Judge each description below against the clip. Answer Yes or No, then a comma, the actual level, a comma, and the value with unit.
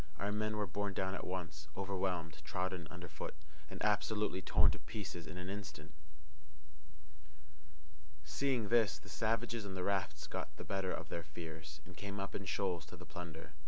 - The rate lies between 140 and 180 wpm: Yes, average, 175 wpm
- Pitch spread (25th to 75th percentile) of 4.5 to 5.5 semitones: No, average, 3.5 semitones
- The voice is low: Yes, very low, 95 Hz